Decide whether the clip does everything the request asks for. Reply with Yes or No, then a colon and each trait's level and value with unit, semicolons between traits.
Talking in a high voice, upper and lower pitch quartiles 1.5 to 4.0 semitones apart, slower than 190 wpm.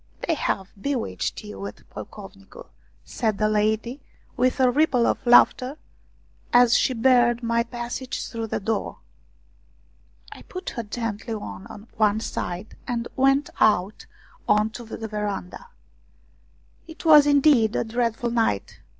Yes: high, 230 Hz; average, 3.2 semitones; average, 140 wpm